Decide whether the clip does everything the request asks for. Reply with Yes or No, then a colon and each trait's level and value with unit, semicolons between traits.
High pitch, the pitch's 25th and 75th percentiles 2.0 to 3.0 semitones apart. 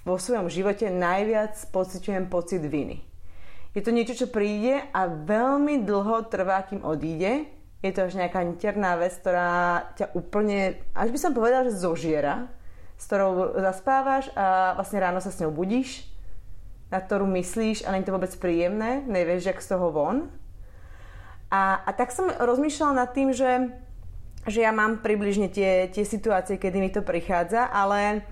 No: high, 195 Hz; average, 4.0 semitones